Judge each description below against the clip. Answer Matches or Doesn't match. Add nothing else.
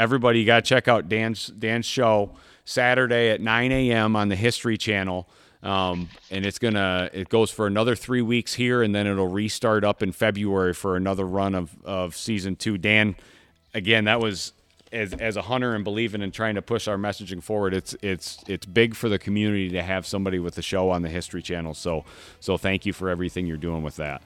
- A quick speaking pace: Matches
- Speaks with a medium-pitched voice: Doesn't match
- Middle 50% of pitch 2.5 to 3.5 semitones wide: Matches